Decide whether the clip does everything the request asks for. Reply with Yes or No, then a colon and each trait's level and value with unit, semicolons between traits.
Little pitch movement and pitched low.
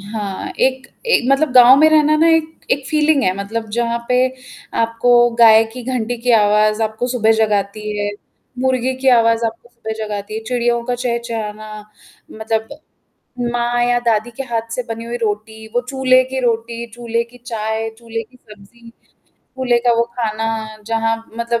No: narrow, 2.0 semitones; high, 235 Hz